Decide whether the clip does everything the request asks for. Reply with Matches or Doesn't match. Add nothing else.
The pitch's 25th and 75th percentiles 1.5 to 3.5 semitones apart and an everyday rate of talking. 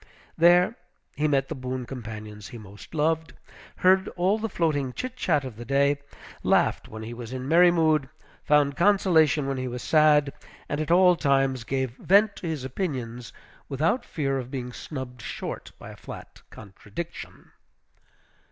Doesn't match